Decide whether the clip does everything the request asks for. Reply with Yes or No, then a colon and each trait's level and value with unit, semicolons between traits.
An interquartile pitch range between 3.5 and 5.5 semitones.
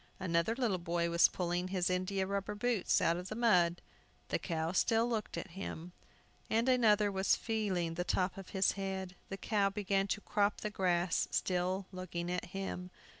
No: narrow, 2.5 semitones